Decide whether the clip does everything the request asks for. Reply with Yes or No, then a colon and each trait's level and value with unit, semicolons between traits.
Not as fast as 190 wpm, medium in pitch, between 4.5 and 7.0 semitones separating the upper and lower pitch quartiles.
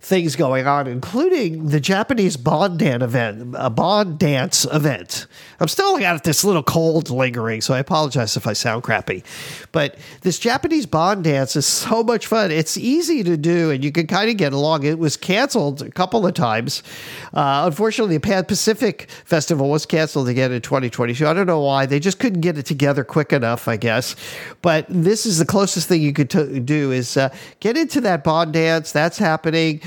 No: average, 200 wpm; medium, 160 Hz; average, 5.3 semitones